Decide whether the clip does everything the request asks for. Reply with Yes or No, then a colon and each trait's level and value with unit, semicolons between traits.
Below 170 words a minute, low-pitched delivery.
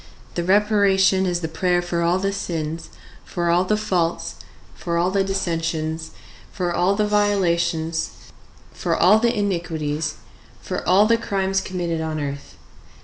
No: average, 145 wpm; medium, 175 Hz